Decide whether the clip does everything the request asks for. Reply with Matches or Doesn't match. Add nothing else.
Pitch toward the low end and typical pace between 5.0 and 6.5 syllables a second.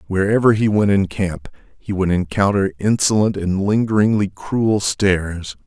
Doesn't match